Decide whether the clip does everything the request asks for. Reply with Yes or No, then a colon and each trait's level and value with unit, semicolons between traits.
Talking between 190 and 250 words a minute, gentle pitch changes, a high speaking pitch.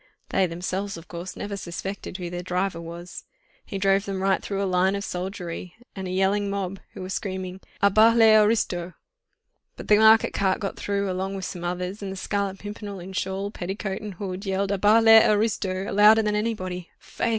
Yes: average, 200 wpm; narrow, 1.8 semitones; high, 195 Hz